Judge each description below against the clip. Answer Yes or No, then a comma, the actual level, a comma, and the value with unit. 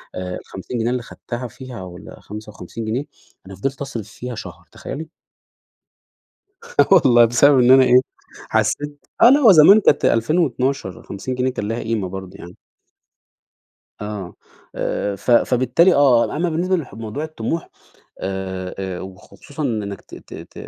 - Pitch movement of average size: No, wide, 5.9 semitones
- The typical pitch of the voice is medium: No, low, 120 Hz